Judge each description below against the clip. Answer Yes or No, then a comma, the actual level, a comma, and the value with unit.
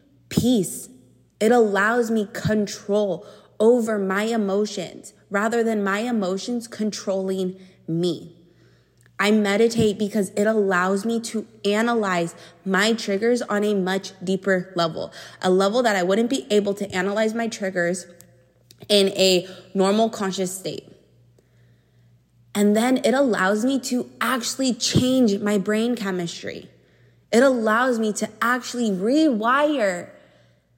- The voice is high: Yes, high, 205 Hz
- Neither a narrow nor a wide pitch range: Yes, average, 3.5 semitones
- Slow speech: Yes, slow, 120 wpm